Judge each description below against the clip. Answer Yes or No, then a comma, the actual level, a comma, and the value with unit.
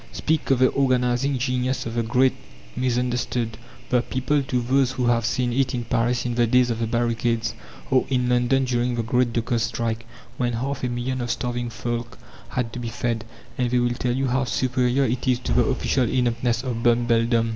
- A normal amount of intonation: No, narrow, 1.4 semitones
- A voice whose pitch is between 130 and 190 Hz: No, low, 120 Hz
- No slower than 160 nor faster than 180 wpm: No, average, 200 wpm